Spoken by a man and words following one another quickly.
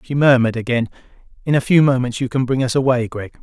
Yes: male; fast, 230 wpm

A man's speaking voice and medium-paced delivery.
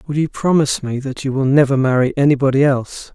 No: male; fast, 210 wpm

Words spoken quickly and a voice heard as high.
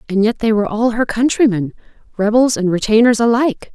No: average, 160 wpm; high, 220 Hz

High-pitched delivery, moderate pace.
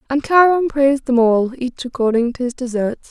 Yes: very high, 260 Hz; average, 195 wpm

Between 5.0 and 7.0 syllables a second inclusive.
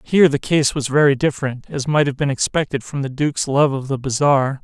Yes: 6.0 syllables/s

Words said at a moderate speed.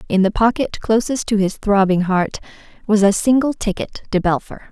Yes: average, 180 wpm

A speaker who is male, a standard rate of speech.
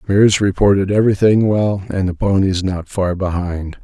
Yes: male; average, 155 wpm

